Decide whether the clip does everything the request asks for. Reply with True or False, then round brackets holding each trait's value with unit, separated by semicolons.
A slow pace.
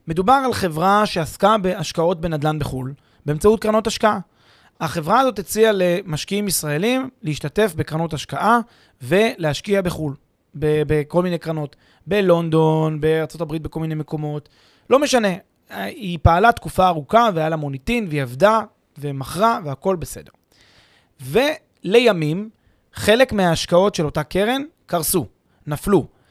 False (115 wpm)